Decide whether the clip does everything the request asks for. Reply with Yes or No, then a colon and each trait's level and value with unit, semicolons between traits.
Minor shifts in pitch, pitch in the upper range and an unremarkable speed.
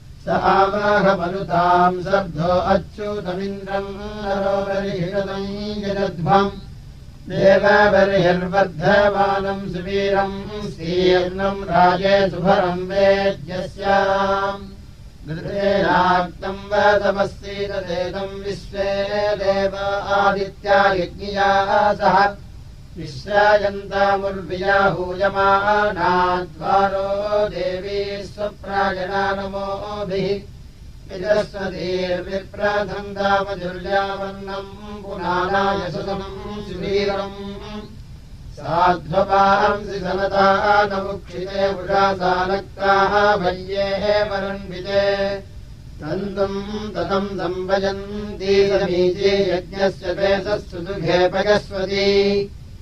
No: narrow, 1.3 semitones; high, 195 Hz; slow, 40 wpm